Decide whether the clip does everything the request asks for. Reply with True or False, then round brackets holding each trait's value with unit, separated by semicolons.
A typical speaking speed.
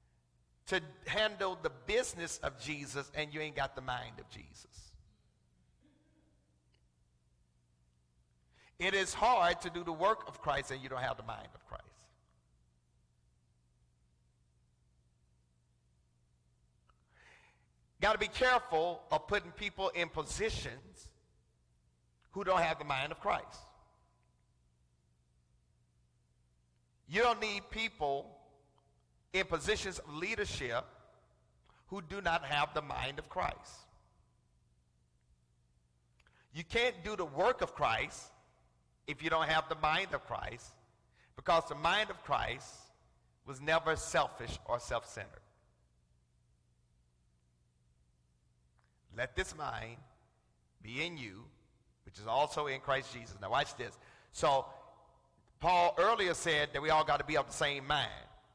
False (120 wpm)